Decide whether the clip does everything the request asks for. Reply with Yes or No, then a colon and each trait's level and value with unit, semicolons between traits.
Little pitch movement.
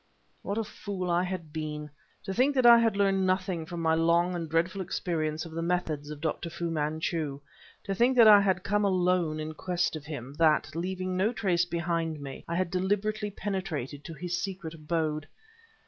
No: average, 3.3 semitones